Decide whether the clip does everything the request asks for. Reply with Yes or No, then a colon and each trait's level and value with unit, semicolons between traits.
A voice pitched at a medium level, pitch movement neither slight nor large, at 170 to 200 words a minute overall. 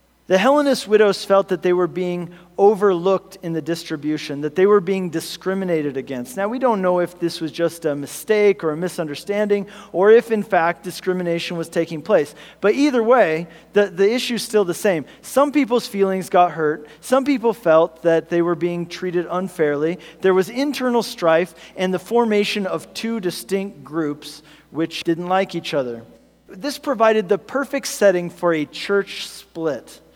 Yes: medium, 180 Hz; average, 3.8 semitones; average, 175 wpm